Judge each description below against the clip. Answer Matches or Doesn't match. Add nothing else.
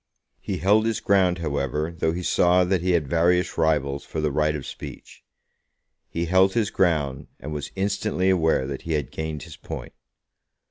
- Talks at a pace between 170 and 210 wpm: Matches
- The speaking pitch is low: Matches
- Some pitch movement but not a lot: Matches